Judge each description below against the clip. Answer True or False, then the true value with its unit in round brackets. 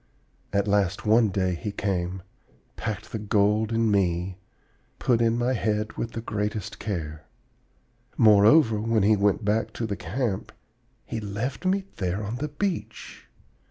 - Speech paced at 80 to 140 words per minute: False (155 wpm)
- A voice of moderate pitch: False (105 Hz)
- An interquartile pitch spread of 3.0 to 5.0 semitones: False (2.4 semitones)